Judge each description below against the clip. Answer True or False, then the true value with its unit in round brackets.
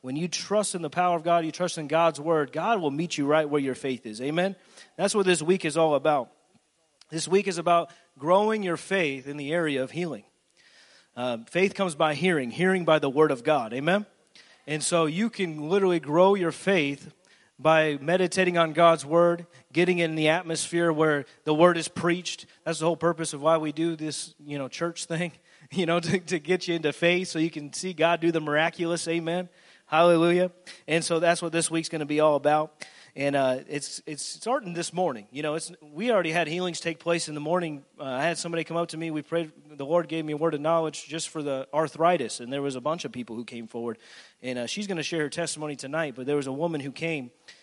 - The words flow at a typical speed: False (235 wpm)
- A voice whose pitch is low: False (165 Hz)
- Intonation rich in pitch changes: False (2.5 semitones)